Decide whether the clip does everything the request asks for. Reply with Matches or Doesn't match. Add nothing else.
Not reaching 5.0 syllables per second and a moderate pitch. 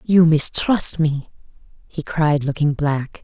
Matches